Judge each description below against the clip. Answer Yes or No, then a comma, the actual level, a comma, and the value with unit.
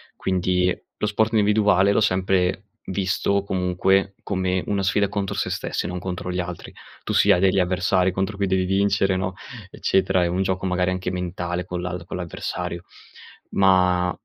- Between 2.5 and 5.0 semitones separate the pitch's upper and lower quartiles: No, narrow, 1.3 semitones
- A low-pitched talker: Yes, very low, 95 Hz